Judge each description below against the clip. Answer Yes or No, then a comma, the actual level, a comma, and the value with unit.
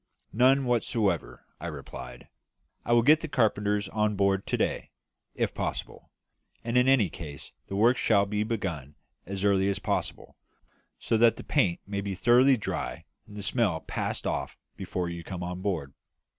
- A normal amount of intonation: Yes, average, 4.6 semitones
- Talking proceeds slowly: No, average, 170 wpm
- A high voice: No, low, 100 Hz